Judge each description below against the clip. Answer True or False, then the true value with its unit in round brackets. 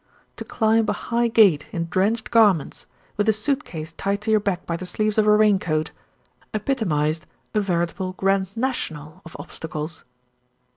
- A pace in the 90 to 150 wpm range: False (165 wpm)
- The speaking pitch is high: True (195 Hz)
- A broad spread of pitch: False (4.7 semitones)